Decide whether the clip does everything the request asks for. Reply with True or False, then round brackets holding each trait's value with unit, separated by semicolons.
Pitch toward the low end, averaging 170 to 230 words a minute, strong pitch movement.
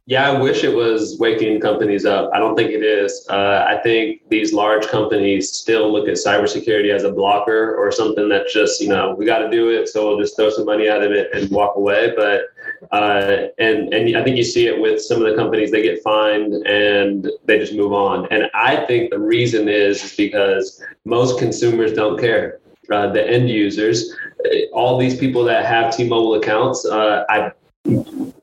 True (115 Hz; 205 wpm; 8.8 semitones)